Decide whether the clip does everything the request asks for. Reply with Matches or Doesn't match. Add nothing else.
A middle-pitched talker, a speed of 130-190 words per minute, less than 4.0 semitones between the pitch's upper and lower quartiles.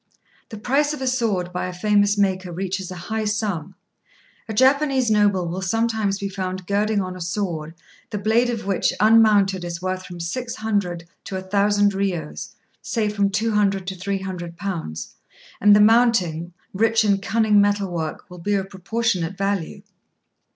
Doesn't match